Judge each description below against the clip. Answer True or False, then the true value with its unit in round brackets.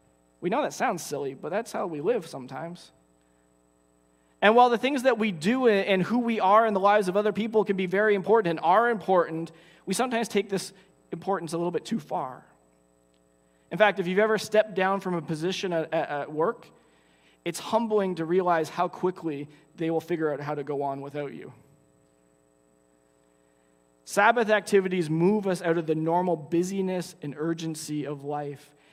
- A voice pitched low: False (165 Hz)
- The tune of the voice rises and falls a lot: True (7.0 semitones)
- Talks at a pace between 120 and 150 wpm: False (180 wpm)